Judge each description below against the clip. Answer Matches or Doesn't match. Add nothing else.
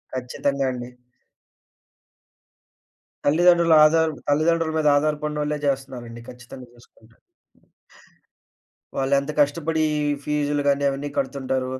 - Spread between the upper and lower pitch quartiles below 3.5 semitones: Matches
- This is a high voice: Doesn't match